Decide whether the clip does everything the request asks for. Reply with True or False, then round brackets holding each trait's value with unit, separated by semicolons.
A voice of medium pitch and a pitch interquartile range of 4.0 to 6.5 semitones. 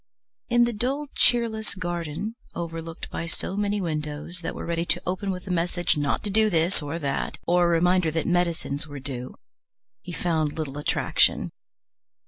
False (170 Hz; 3.4 semitones)